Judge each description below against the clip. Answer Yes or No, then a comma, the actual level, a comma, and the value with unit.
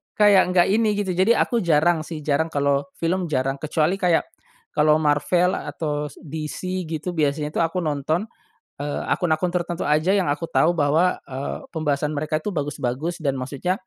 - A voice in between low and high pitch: Yes, medium, 155 Hz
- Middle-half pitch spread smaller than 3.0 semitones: No, average, 3.3 semitones